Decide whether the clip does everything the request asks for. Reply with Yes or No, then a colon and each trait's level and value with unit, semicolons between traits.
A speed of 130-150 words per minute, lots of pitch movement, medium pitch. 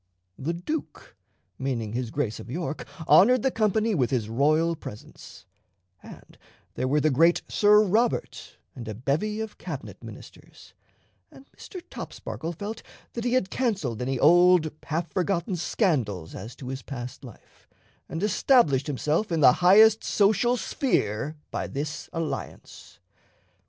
Yes: average, 140 wpm; wide, 8.0 semitones; medium, 165 Hz